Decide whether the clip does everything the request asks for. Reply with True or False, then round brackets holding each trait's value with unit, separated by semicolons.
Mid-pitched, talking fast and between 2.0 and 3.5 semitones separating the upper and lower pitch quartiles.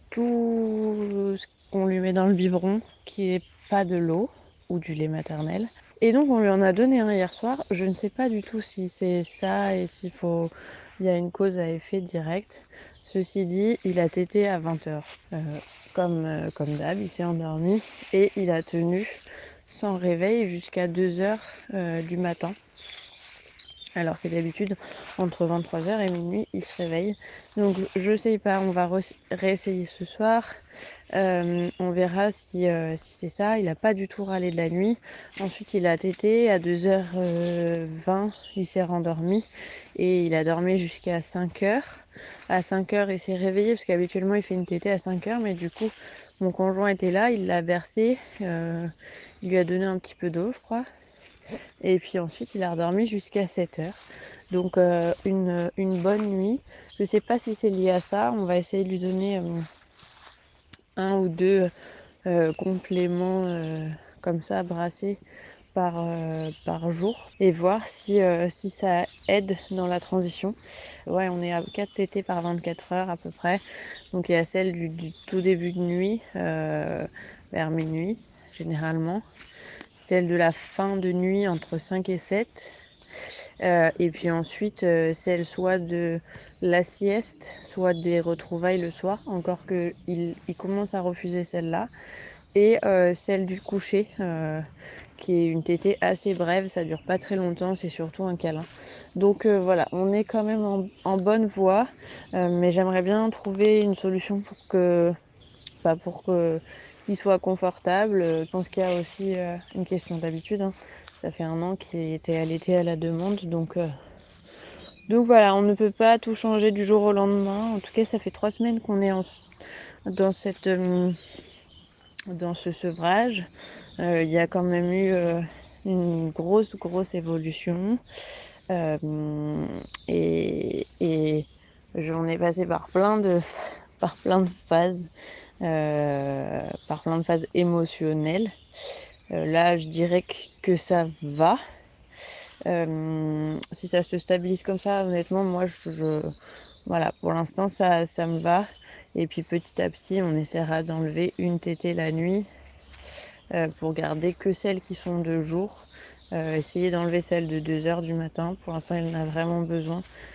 False (180 Hz; 175 wpm; 2.6 semitones)